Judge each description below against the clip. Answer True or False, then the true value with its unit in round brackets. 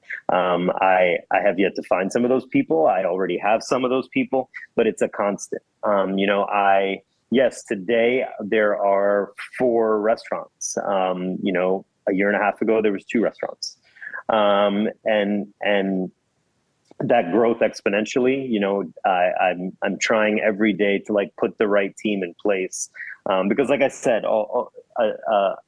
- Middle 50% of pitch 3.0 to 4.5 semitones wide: False (2.6 semitones)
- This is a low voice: True (105 Hz)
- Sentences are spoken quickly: False (180 wpm)